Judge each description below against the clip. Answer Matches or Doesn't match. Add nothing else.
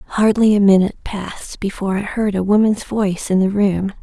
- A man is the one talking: Doesn't match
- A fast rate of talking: Doesn't match